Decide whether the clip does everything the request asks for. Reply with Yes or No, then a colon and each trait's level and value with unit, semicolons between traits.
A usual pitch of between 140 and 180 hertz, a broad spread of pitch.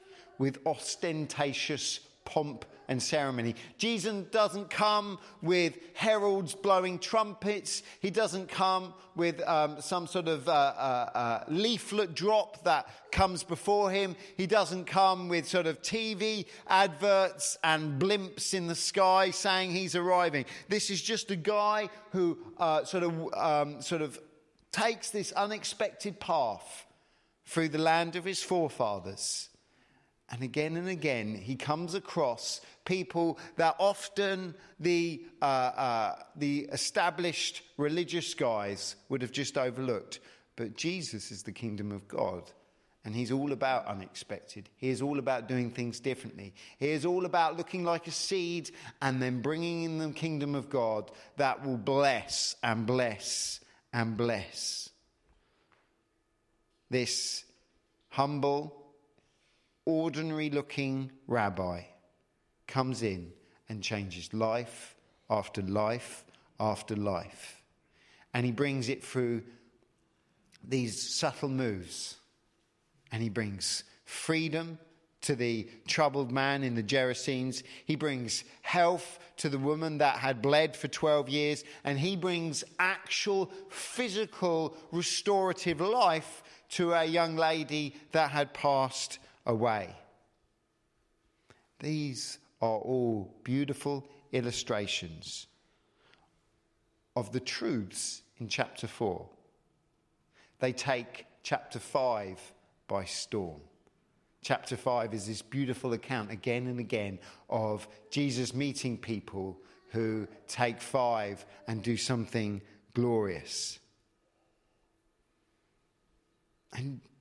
Yes: medium, 145 Hz; wide, 6.6 semitones